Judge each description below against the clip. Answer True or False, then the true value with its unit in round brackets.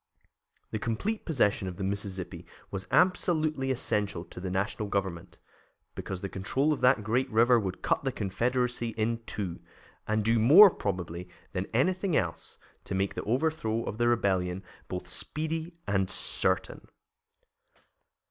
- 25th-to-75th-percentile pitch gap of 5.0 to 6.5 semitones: True (5.5 semitones)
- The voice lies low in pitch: True (110 Hz)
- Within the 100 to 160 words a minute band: True (145 wpm)